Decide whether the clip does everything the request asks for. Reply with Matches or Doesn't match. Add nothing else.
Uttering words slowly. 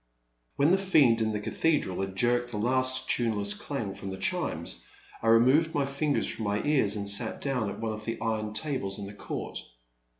Doesn't match